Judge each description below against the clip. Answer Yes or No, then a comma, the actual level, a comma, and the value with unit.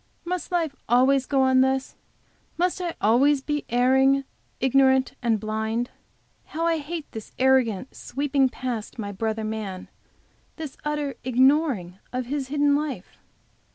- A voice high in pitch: Yes, very high, 265 Hz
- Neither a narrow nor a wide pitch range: Yes, average, 3.8 semitones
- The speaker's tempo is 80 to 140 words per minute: Yes, slow, 135 wpm